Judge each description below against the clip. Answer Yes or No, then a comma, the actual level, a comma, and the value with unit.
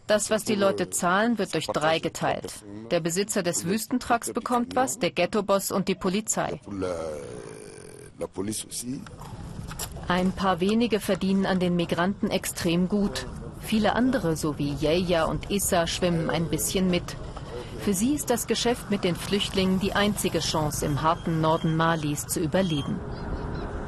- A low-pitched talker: No, medium, 185 Hz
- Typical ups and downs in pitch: Yes, average, 3.9 semitones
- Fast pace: No, average, 145 wpm